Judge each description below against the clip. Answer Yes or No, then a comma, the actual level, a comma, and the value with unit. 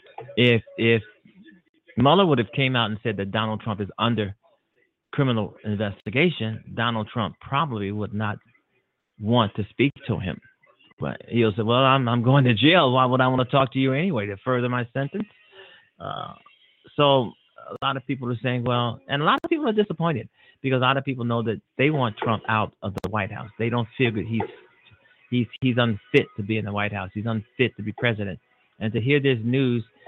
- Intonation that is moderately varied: Yes, average, 3.5 semitones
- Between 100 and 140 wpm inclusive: No, fast, 205 wpm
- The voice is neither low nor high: No, low, 120 Hz